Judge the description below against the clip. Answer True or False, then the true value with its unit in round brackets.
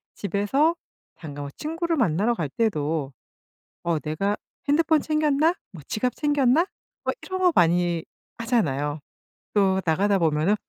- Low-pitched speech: False (205 Hz)